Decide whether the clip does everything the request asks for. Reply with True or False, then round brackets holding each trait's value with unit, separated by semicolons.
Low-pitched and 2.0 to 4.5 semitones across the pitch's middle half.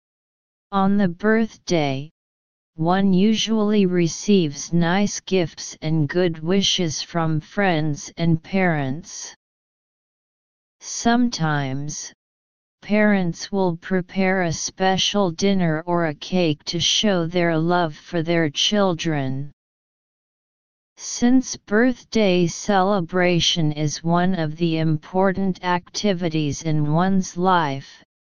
False (175 Hz; 3.6 semitones)